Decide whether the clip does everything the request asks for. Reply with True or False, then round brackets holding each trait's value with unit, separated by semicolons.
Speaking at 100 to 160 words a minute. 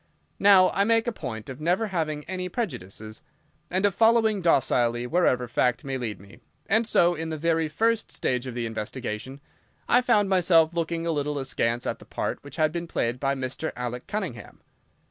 False (185 wpm)